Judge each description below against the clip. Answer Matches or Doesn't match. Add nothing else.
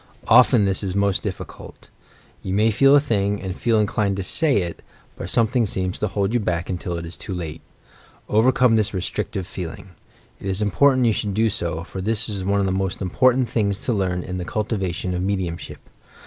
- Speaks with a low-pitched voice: Matches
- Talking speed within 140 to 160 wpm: Doesn't match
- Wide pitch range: Doesn't match